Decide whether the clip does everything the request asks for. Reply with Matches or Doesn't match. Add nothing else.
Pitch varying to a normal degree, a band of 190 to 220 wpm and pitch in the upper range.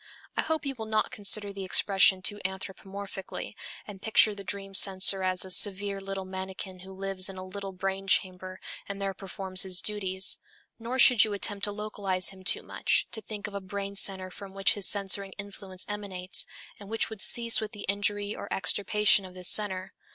Doesn't match